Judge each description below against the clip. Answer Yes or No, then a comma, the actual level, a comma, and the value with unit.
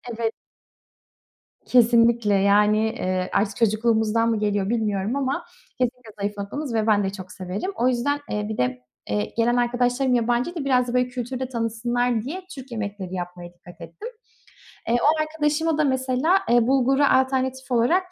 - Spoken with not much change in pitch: No, average, 3.9 semitones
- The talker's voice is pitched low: No, high, 235 Hz